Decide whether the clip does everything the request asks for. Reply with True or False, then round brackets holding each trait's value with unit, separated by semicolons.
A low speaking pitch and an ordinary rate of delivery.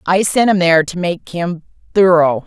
False (175 Hz; 195 wpm)